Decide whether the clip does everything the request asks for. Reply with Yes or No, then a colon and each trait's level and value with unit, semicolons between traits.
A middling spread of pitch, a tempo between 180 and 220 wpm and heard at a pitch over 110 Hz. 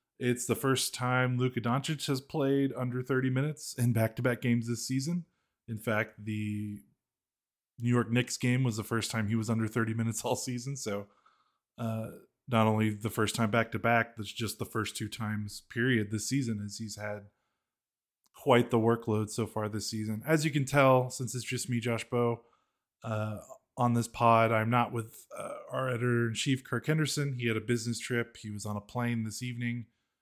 No: narrow, 2.2 semitones; average, 190 wpm; low, 120 Hz